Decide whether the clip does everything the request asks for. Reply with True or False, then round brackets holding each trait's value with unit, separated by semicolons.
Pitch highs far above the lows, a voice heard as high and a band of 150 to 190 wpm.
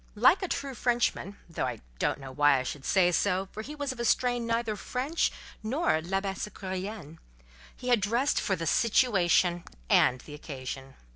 True (6.5 semitones; 200 Hz; 165 wpm)